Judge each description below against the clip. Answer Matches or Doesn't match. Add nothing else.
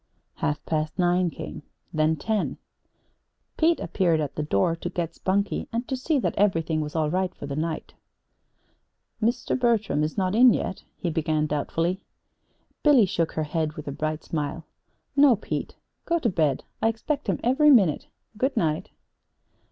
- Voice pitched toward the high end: Doesn't match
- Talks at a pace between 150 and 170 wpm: Matches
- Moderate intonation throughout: Doesn't match